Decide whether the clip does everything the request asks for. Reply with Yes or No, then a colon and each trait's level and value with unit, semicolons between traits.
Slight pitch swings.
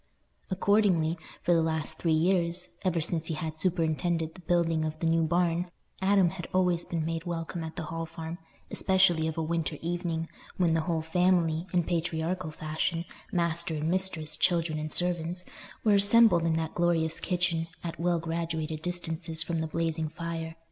Yes: narrow, 1.6 semitones